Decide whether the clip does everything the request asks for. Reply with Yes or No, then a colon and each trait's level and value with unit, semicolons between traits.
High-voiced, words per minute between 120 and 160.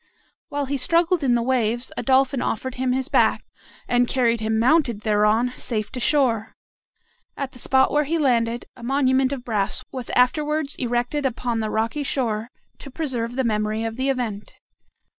No: very high, 250 Hz; average, 175 wpm